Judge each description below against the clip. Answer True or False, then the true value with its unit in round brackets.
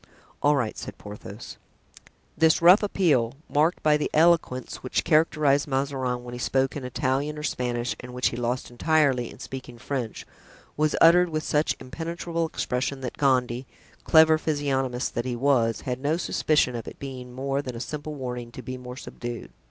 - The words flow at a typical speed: True (175 wpm)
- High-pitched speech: False (135 Hz)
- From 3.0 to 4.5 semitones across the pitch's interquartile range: True (3.5 semitones)